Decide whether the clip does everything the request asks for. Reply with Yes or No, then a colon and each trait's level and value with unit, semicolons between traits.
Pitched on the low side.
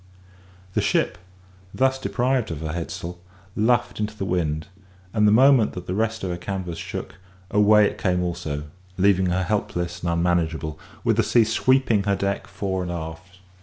Yes: very low, 95 Hz